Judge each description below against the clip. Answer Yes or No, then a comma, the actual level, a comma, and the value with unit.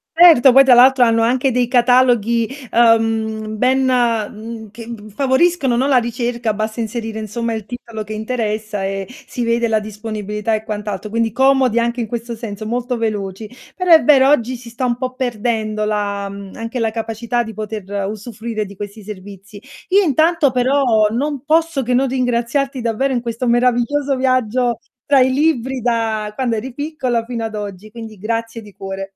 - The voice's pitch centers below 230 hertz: No, high, 235 Hz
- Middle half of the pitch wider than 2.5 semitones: Yes, average, 2.9 semitones